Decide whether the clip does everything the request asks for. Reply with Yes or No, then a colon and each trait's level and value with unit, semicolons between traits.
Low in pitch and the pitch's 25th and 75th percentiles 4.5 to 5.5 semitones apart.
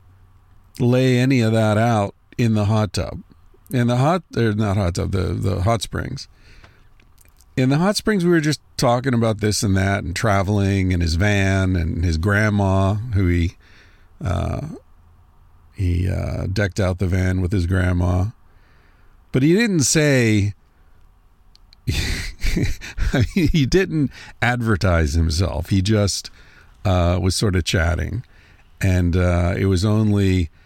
No: very low, 95 Hz; average, 3.9 semitones